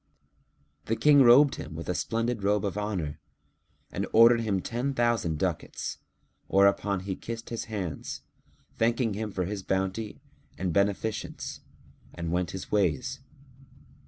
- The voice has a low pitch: Yes, low, 105 Hz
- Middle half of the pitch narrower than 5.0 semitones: Yes, average, 3.6 semitones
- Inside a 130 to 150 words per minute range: Yes, slow, 135 wpm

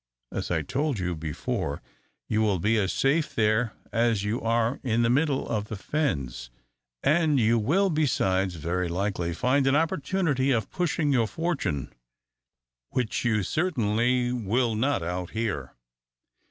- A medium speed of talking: Yes, average, 145 wpm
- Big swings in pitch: Yes, wide, 6.1 semitones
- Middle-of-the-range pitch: No, low, 115 Hz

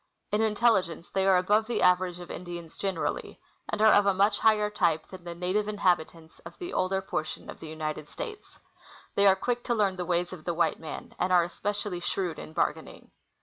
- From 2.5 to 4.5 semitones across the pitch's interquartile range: Yes, average, 3.2 semitones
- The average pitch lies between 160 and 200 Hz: Yes, medium, 185 Hz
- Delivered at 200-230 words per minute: Yes, fast, 205 wpm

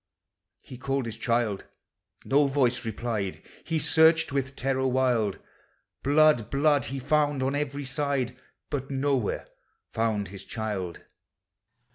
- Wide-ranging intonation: No, average, 3.6 semitones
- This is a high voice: No, low, 130 Hz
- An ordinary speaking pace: No, slow, 130 wpm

